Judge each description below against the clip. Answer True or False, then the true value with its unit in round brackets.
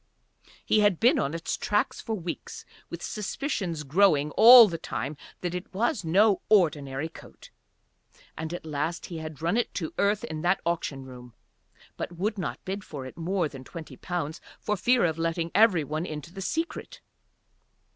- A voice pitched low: False (170 Hz)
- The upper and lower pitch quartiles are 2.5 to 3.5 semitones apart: False (4.5 semitones)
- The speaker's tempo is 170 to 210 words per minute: True (175 wpm)